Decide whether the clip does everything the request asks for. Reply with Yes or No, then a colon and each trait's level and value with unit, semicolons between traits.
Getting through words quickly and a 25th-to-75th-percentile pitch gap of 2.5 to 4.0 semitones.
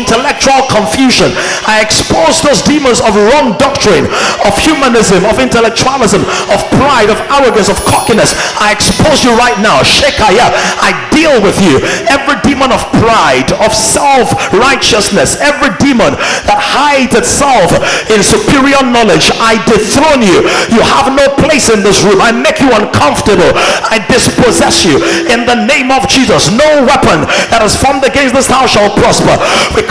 No: average, 155 wpm; average, 3.5 semitones